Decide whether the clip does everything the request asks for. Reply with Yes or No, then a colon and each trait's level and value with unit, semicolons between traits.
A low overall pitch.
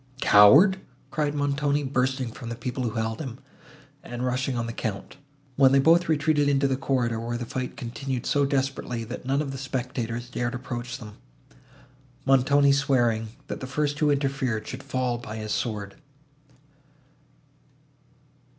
Yes: low, 130 Hz